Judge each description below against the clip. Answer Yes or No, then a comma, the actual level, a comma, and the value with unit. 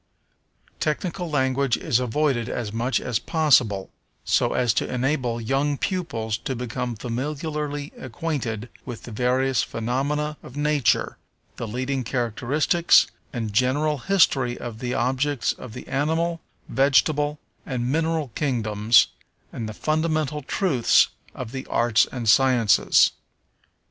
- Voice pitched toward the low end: Yes, low, 130 Hz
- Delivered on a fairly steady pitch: No, average, 4.0 semitones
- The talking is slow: Yes, slow, 125 wpm